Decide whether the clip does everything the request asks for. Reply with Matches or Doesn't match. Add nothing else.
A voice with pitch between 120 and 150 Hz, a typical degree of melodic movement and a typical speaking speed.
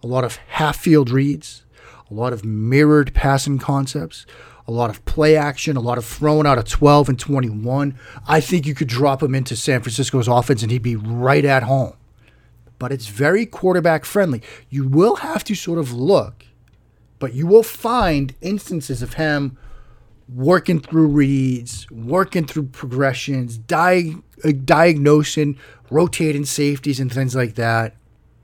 Matches